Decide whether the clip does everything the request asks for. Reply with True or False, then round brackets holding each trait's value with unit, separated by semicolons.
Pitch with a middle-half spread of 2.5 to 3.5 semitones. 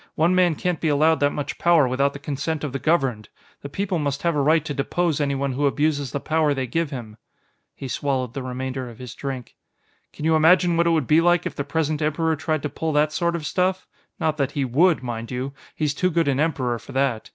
True (3.2 semitones)